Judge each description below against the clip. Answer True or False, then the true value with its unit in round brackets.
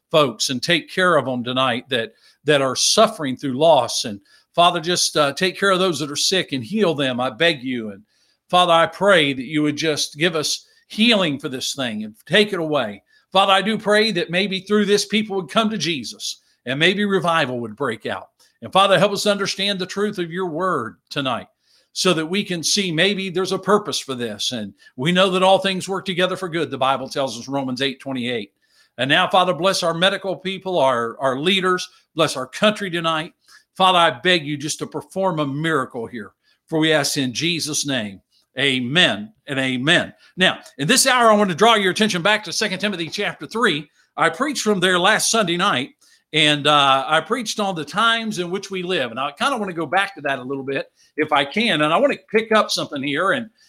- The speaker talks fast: True (220 wpm)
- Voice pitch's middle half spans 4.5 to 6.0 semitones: True (5.2 semitones)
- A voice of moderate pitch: True (180 Hz)